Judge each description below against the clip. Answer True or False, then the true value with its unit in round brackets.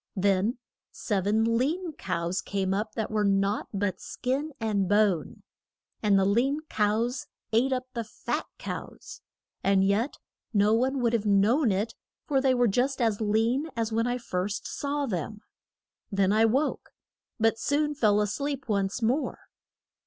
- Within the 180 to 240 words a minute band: False (160 wpm)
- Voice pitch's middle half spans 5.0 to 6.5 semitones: False (4.2 semitones)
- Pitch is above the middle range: True (220 Hz)